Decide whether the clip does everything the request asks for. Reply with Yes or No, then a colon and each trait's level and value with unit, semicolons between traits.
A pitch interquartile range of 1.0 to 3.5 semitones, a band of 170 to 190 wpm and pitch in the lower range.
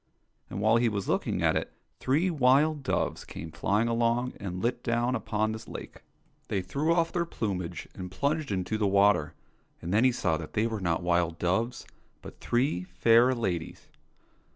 No: wide, 5.5 semitones; average, 175 wpm; low, 110 Hz